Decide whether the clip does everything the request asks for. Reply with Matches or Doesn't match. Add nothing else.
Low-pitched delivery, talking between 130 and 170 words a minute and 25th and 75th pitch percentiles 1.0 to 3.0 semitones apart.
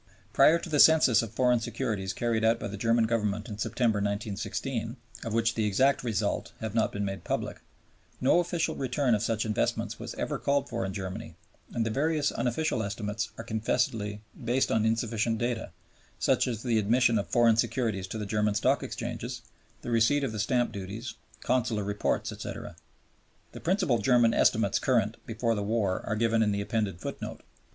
Doesn't match